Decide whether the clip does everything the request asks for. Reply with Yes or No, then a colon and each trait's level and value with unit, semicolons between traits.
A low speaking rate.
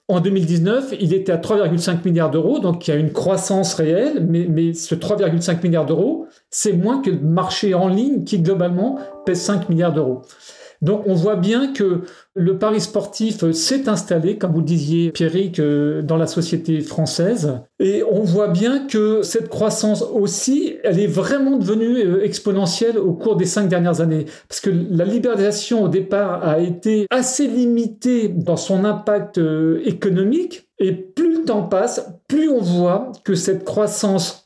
No: average, 170 wpm